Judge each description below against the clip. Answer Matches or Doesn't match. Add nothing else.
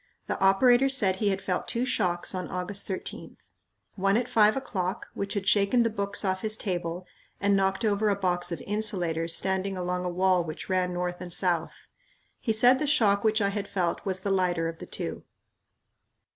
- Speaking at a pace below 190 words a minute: Doesn't match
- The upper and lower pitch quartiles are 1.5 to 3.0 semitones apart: Matches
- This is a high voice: Matches